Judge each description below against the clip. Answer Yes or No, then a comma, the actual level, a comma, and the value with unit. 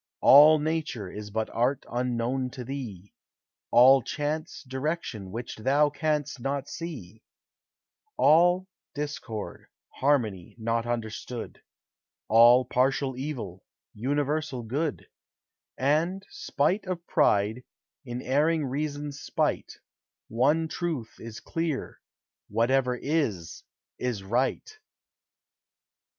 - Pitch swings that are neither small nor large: Yes, average, 4.5 semitones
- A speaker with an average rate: No, slow, 95 wpm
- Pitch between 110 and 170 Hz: Yes, low, 135 Hz